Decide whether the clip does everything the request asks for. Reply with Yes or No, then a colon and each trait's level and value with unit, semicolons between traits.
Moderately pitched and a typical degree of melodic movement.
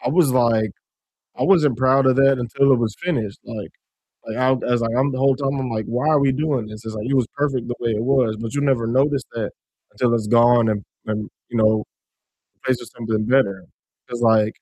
No: low, 120 Hz; average, 3.4 semitones